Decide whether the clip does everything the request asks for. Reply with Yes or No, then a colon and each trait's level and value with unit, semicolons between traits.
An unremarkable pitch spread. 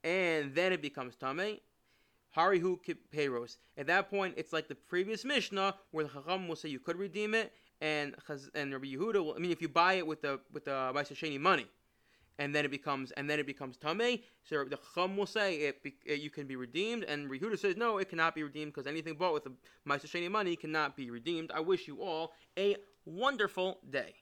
Yes: average, 4.6 semitones